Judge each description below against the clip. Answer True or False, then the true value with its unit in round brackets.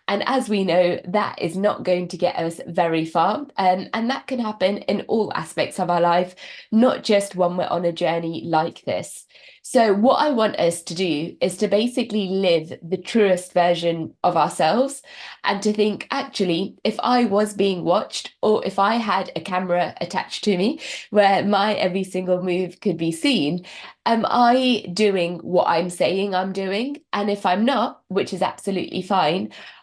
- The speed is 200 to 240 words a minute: False (185 wpm)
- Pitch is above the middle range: True (195 Hz)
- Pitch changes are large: False (3.3 semitones)